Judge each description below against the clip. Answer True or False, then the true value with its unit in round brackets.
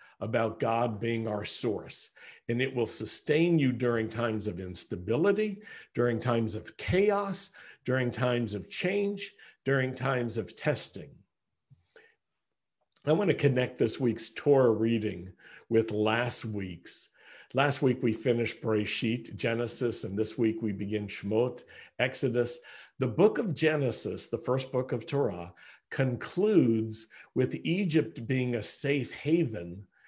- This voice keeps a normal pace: False (130 wpm)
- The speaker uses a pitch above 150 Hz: False (120 Hz)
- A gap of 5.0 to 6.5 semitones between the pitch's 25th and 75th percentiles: False (4.0 semitones)